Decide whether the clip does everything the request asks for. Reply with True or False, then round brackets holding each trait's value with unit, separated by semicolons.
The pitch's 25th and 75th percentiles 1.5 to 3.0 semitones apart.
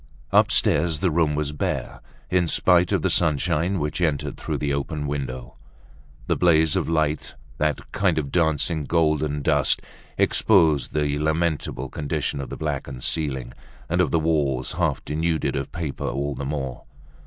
True (2.5 semitones)